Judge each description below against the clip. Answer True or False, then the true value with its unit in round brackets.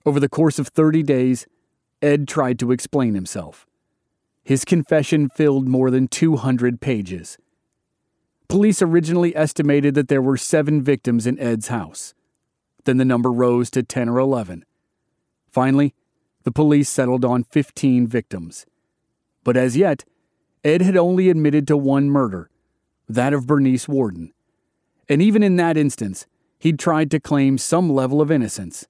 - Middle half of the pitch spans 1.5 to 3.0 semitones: False (3.7 semitones)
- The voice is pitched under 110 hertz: False (140 Hz)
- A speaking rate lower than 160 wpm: True (145 wpm)